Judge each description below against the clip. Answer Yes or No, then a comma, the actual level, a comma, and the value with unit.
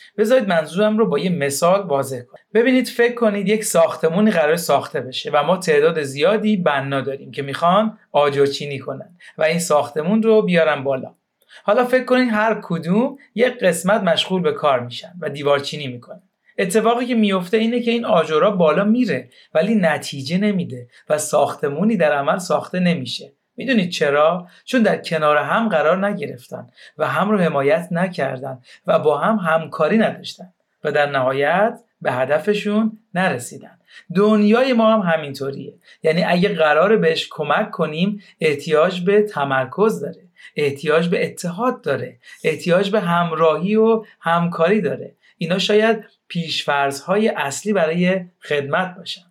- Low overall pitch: No, medium, 185 Hz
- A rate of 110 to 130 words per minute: No, average, 145 wpm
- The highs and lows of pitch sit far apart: Yes, wide, 6.0 semitones